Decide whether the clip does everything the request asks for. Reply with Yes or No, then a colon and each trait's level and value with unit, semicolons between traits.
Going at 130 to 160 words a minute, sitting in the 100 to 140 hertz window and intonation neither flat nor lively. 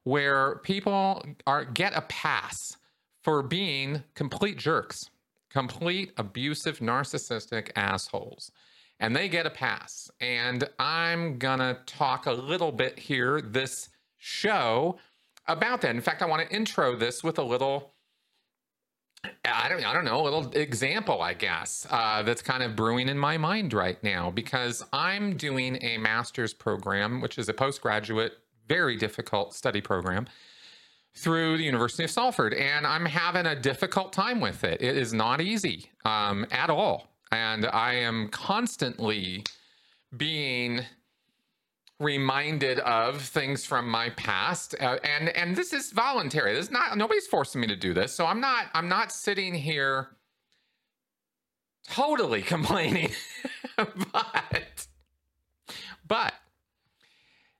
No: slow, 135 wpm; low, 135 Hz; wide, 5.9 semitones